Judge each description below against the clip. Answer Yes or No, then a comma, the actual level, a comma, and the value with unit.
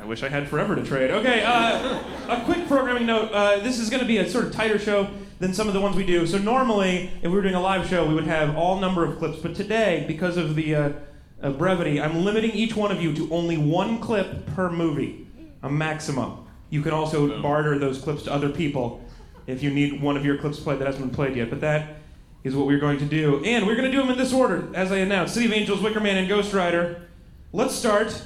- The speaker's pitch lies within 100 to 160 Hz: No, medium, 175 Hz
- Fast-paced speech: Yes, fast, 255 wpm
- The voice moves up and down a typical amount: No, wide, 6.1 semitones